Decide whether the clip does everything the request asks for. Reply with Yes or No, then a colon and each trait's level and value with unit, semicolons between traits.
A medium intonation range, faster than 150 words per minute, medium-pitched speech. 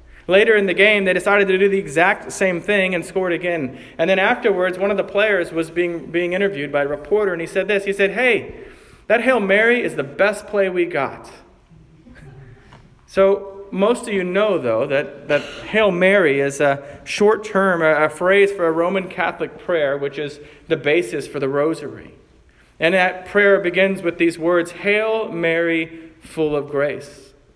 Yes: average, 5.0 semitones; average, 185 wpm; medium, 180 Hz